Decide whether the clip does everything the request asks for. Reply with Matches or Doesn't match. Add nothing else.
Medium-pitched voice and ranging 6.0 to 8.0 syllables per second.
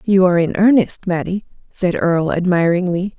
Doesn't match